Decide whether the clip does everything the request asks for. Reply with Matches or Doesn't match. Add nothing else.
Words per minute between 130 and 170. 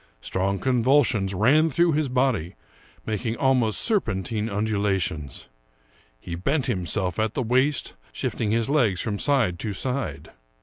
Matches